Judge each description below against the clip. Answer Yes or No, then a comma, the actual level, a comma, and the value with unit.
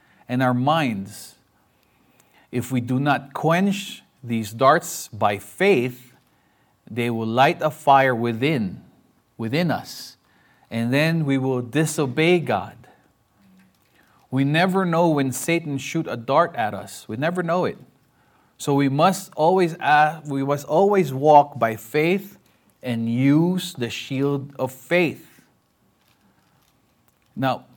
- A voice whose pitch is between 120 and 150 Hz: Yes, medium, 140 Hz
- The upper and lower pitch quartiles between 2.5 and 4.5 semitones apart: No, average, 5.1 semitones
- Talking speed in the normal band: No, slow, 125 wpm